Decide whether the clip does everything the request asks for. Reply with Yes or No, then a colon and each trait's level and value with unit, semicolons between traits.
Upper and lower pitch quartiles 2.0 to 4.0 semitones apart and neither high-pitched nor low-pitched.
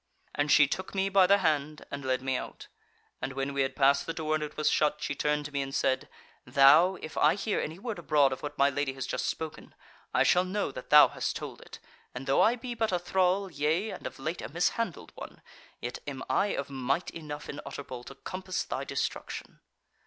No: average, 4.8 semitones; medium, 150 Hz